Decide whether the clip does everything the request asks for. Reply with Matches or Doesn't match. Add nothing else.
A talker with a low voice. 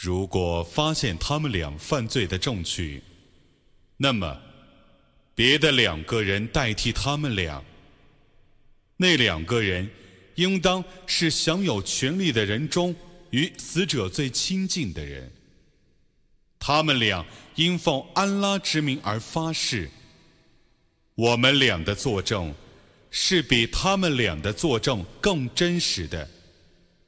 Matches